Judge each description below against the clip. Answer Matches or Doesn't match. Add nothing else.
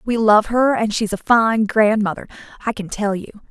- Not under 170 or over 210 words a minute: Matches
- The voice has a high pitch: Matches